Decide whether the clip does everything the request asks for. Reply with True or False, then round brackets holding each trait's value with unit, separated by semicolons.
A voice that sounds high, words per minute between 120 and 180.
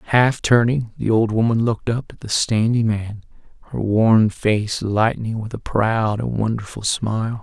False (110 Hz; 170 wpm)